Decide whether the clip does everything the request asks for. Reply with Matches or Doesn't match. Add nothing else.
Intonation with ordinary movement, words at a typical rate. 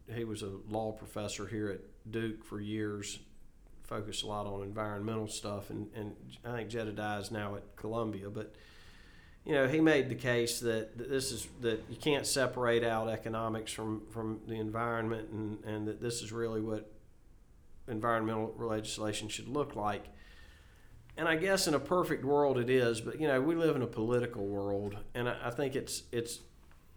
Doesn't match